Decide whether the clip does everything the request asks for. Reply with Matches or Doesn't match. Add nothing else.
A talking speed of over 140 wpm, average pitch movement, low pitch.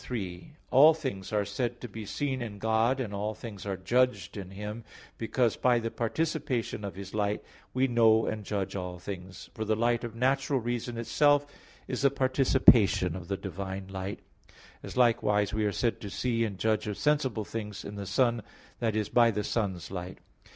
Matches